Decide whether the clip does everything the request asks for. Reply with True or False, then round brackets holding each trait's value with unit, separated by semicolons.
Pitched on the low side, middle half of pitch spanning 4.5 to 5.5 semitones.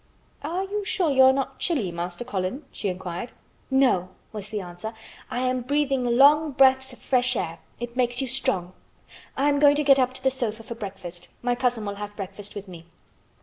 False (245 Hz; 5.1 semitones)